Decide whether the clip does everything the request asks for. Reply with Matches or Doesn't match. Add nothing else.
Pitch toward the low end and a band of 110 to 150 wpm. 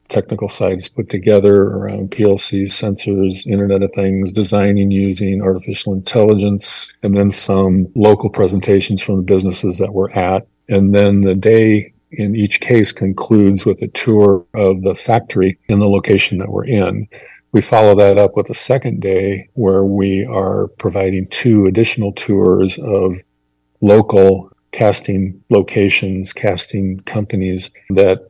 Matches